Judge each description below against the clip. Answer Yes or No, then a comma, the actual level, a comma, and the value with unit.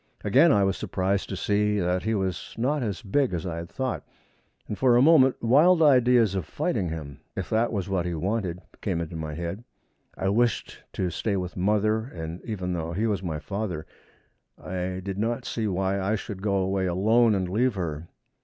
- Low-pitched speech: Yes, low, 100 Hz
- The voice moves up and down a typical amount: Yes, average, 4.0 semitones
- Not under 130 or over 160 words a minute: No, average, 200 wpm